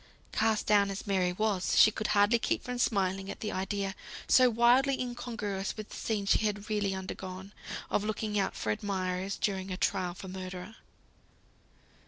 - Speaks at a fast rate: No, average, 170 wpm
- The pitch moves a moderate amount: No, narrow, 2.3 semitones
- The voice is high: Yes, high, 200 Hz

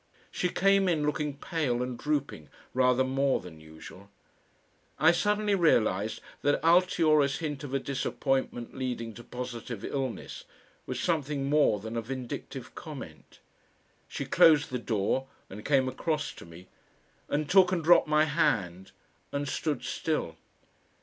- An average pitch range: Yes, average, 4.5 semitones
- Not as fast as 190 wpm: Yes, average, 140 wpm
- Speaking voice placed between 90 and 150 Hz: Yes, low, 135 Hz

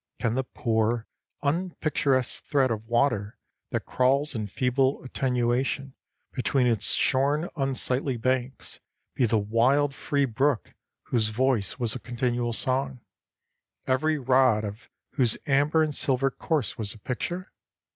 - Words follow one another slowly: Yes, slow, 130 wpm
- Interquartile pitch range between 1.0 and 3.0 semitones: Yes, average, 2.7 semitones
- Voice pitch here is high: No, low, 130 Hz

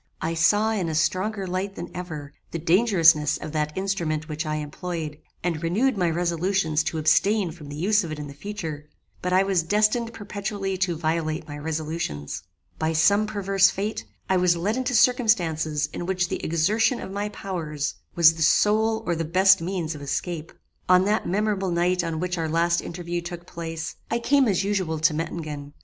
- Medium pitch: Yes, medium, 175 Hz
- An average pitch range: Yes, average, 3.8 semitones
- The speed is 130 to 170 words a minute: No, average, 185 wpm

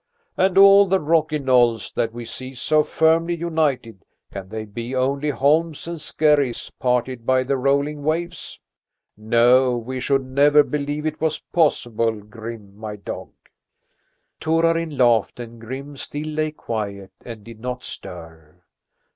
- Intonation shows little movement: No, average, 4.9 semitones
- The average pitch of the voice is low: Yes, low, 130 Hz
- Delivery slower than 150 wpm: Yes, average, 140 wpm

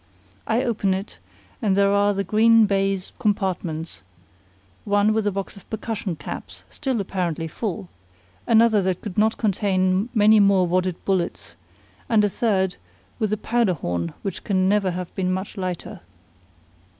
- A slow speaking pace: No, average, 150 wpm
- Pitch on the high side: Yes, high, 195 Hz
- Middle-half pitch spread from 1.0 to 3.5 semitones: Yes, narrow, 2.6 semitones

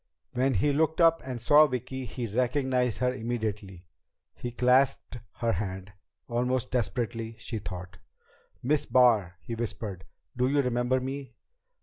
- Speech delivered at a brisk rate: No, slow, 135 wpm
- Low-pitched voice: Yes, low, 125 Hz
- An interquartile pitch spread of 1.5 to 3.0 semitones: Yes, average, 2.7 semitones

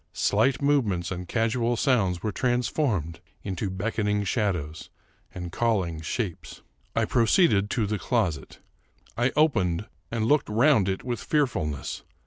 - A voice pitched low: Yes, low, 105 Hz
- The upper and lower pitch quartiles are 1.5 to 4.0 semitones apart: No, average, 5.1 semitones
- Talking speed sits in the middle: No, slow, 125 wpm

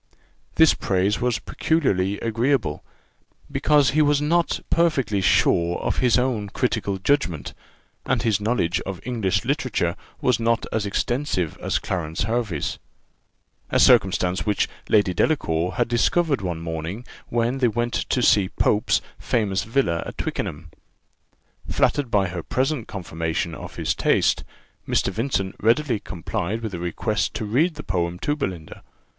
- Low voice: Yes, low, 110 Hz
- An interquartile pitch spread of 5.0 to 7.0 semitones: Yes, wide, 5.5 semitones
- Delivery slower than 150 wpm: Yes, average, 140 wpm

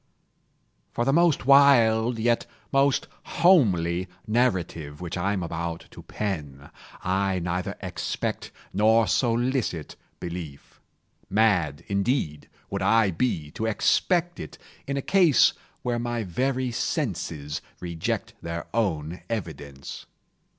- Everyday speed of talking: No, slow, 115 wpm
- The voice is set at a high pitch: No, low, 105 Hz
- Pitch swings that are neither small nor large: No, wide, 6.6 semitones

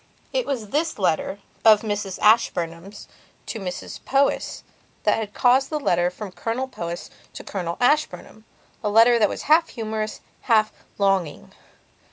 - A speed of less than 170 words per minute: Yes, average, 140 wpm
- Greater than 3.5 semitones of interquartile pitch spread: Yes, average, 4.4 semitones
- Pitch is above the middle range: Yes, high, 215 Hz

